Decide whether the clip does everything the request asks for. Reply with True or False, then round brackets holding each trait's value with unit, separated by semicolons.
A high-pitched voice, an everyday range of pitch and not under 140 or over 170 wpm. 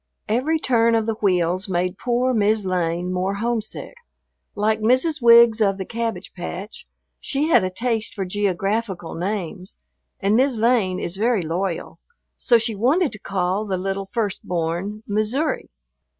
True (210 Hz; 3.9 semitones; 150 wpm)